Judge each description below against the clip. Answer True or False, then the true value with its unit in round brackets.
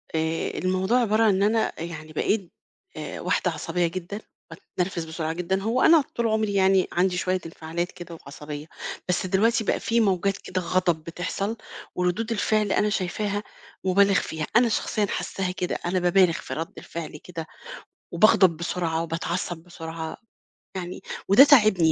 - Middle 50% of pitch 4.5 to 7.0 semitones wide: False (3.4 semitones)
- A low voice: False (185 Hz)